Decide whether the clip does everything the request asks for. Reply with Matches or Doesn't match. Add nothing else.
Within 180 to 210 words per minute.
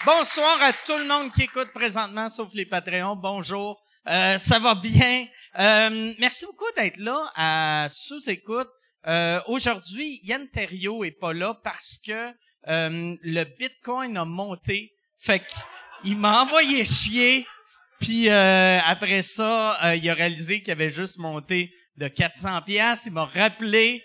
Doesn't match